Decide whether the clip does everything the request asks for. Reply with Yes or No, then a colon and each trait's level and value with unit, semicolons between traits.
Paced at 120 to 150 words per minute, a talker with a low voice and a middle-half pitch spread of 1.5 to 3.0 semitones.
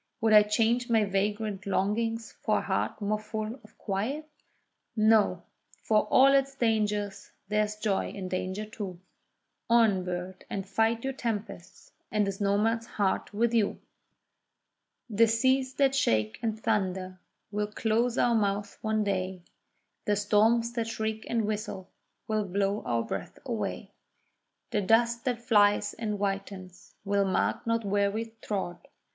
No: average, 145 wpm; high, 210 Hz; narrow, 2.4 semitones